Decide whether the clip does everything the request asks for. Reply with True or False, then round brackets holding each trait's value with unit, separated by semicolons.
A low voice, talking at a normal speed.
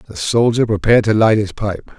False (105 Hz; 210 wpm)